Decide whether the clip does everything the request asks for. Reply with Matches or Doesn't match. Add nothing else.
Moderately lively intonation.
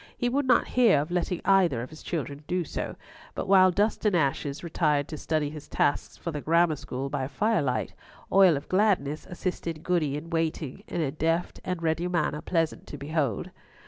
Matches